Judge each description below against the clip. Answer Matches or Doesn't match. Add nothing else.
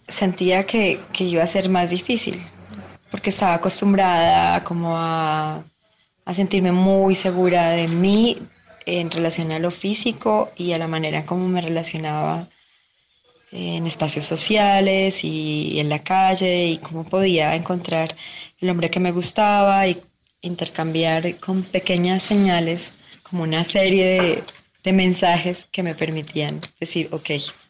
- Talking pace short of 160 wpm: Matches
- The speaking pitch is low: Doesn't match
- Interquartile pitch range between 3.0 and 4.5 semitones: Doesn't match